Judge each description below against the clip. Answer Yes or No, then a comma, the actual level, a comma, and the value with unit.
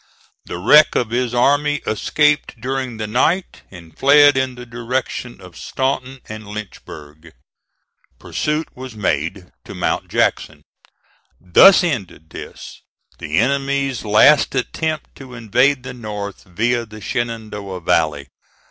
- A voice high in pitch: No, low, 120 Hz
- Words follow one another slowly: Yes, slow, 125 wpm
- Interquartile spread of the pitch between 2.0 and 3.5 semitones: No, average, 5.0 semitones